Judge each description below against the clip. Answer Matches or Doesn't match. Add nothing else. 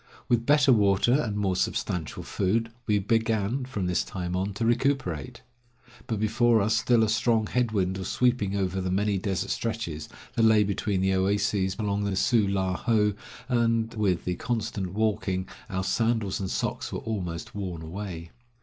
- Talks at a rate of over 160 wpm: Matches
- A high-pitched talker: Doesn't match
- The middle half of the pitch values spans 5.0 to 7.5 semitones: Doesn't match